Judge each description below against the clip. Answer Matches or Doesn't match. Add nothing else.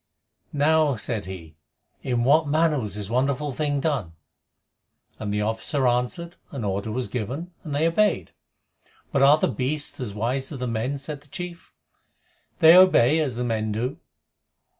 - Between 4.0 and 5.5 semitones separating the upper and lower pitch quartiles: Matches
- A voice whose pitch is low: Matches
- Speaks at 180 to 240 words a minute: Doesn't match